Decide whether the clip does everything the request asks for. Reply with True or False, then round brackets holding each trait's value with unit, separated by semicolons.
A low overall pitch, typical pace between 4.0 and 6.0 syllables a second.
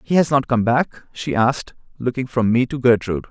True (120 Hz; 5.5 syllables/s)